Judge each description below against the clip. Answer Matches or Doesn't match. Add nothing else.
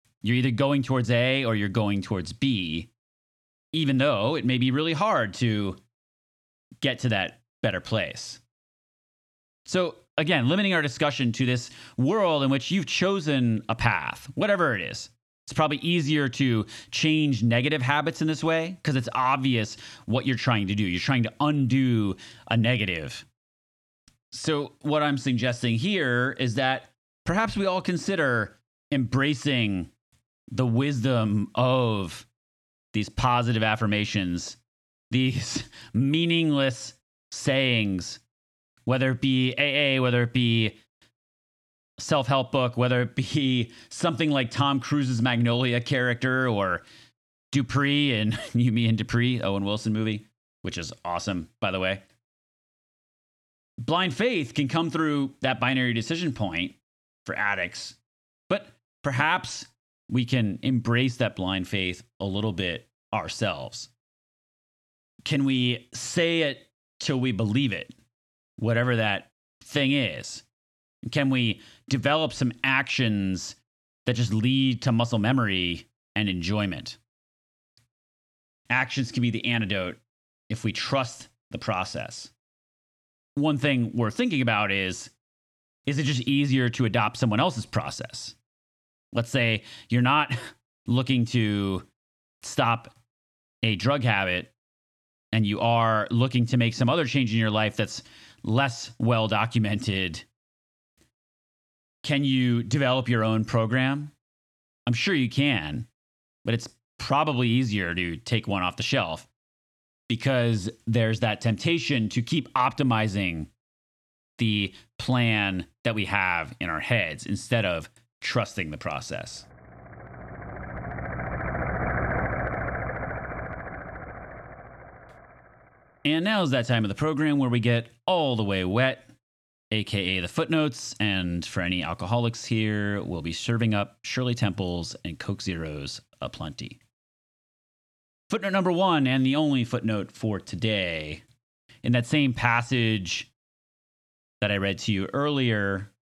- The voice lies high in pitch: Doesn't match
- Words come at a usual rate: Doesn't match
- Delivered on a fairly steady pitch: Doesn't match